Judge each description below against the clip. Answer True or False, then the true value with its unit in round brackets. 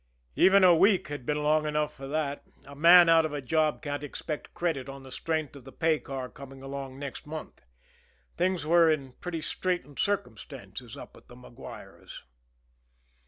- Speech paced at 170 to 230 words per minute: True (175 wpm)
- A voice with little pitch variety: False (3.1 semitones)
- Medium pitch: True (150 Hz)